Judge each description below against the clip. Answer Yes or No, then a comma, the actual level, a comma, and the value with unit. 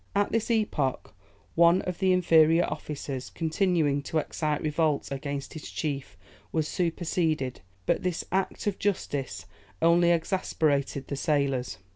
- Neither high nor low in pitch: Yes, medium, 160 Hz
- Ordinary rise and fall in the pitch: Yes, average, 3.7 semitones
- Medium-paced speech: No, slow, 130 wpm